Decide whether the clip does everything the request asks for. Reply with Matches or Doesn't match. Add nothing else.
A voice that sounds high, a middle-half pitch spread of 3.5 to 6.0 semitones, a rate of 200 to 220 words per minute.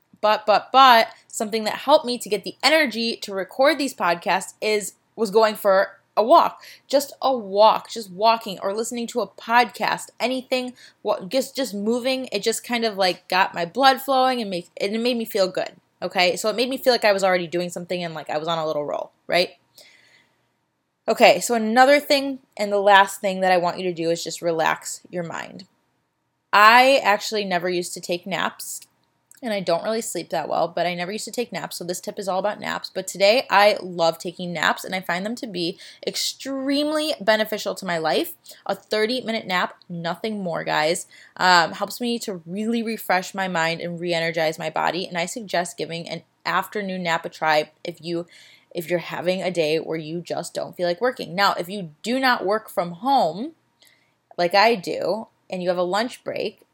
Matches